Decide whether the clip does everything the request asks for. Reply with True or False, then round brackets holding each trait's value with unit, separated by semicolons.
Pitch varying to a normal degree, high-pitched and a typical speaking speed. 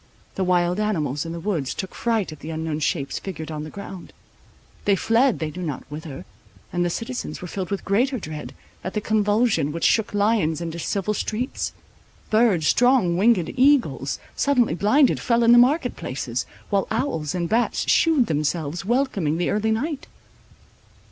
False (6.4 semitones; 195 Hz; 170 wpm)